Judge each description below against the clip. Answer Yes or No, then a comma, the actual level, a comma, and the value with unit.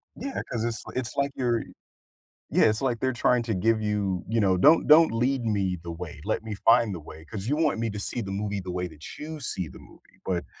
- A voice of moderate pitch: No, low, 110 Hz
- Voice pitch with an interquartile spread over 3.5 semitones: Yes, average, 4.7 semitones